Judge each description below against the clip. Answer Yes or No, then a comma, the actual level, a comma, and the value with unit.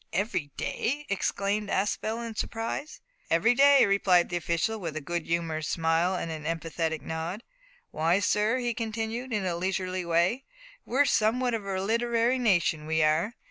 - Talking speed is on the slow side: No, average, 165 wpm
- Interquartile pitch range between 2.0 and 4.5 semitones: No, wide, 5.4 semitones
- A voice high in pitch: Yes, high, 195 Hz